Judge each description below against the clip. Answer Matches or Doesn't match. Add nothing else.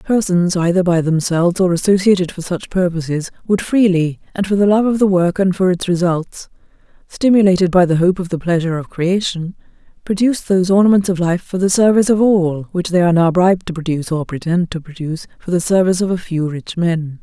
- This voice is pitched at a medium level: Matches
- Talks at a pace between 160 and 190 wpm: Doesn't match